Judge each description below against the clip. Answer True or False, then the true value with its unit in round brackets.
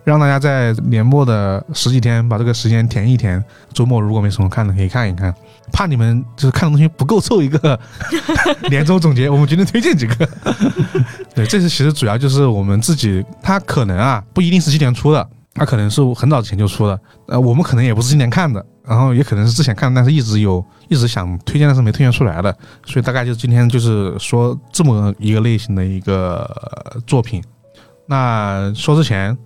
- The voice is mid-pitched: False (120 Hz)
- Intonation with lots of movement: False (4.7 semitones)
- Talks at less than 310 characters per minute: False (325 characters per minute)